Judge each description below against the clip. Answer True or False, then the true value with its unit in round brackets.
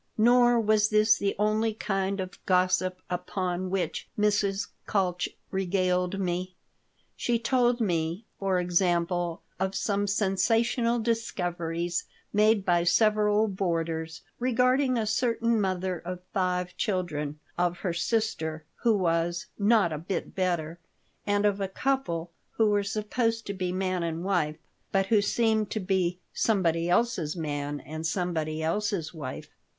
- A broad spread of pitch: False (3.5 semitones)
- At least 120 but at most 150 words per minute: True (135 wpm)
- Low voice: False (190 Hz)